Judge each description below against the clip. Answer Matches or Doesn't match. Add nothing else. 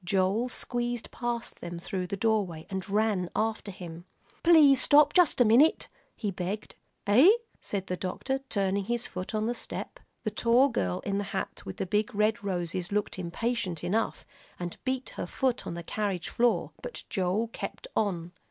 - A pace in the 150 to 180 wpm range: Matches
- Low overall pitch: Doesn't match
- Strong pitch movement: Doesn't match